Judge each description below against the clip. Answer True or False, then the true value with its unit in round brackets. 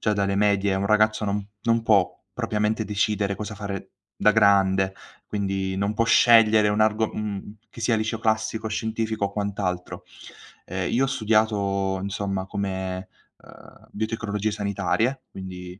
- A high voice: False (105 Hz)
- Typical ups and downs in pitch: False (1.9 semitones)